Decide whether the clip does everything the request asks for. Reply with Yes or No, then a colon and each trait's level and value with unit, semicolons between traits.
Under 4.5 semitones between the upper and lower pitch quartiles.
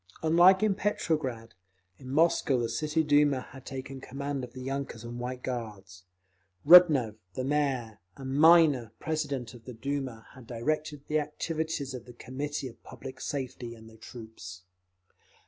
Yes: average, 3.9 semitones